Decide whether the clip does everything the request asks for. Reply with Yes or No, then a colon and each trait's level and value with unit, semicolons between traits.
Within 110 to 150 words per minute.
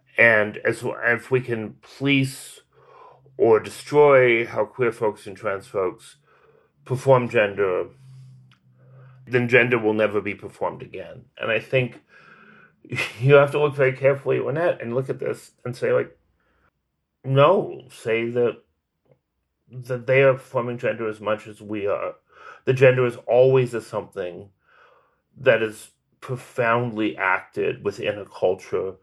Yes: average, 140 wpm